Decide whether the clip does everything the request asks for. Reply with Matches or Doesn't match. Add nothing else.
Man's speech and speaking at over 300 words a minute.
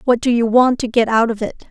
Doesn't match